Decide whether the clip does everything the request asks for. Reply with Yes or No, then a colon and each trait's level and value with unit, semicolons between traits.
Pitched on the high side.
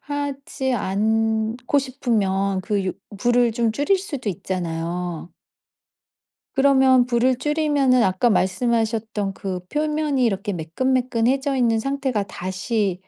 Yes: high, 235 Hz